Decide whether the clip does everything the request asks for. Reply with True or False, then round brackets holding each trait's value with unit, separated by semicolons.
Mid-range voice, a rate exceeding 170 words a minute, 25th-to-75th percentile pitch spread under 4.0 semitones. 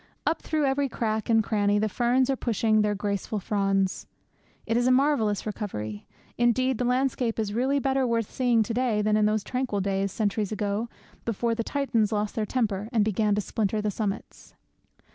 False (220 Hz; 185 wpm; 3.1 semitones)